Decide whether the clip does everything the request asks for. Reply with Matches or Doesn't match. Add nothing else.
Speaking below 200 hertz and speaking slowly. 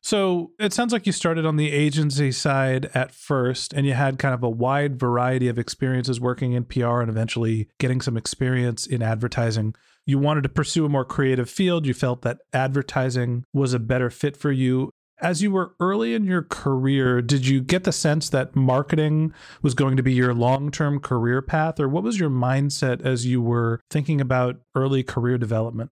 Doesn't match